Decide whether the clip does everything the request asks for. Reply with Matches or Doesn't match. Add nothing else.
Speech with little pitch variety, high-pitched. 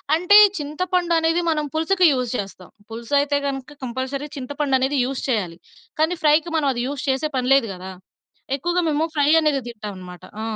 Doesn't match